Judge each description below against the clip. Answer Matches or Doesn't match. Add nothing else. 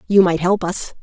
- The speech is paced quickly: Matches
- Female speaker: Matches